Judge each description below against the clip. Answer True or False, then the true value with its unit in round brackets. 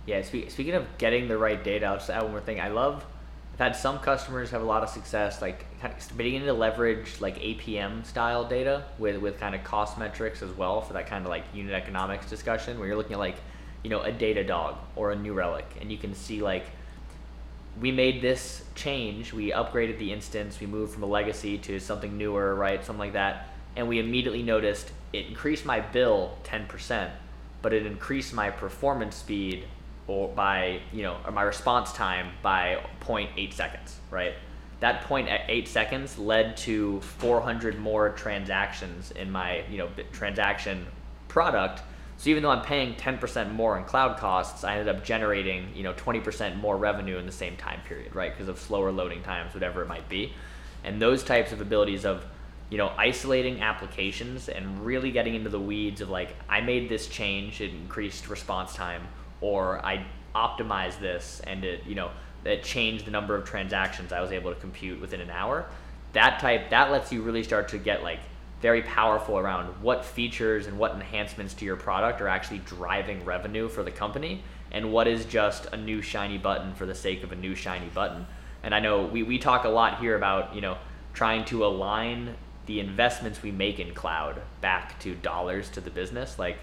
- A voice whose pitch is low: True (105 Hz)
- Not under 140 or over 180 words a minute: False (200 wpm)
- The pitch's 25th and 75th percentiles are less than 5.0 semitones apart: True (3.3 semitones)